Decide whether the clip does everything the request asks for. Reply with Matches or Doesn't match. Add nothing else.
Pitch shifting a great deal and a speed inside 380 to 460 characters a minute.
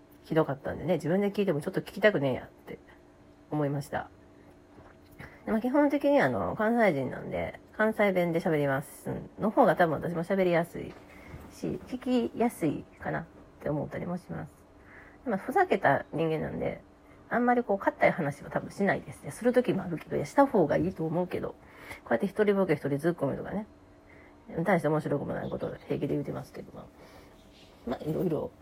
Matches